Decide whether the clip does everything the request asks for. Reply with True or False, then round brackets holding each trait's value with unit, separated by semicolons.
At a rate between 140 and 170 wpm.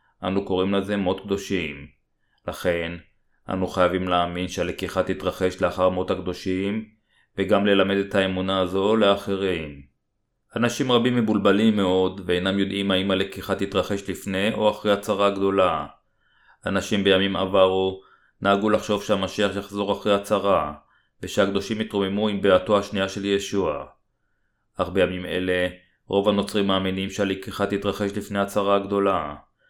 False (125 wpm)